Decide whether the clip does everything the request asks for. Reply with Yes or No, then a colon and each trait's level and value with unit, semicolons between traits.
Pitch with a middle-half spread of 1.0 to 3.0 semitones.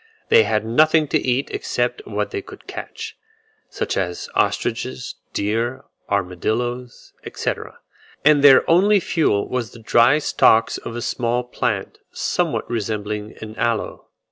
No: average, 5.0 semitones